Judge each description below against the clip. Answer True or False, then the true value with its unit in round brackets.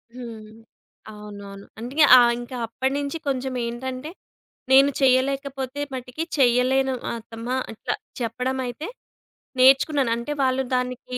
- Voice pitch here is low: False (255 Hz)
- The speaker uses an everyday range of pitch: False (2.1 semitones)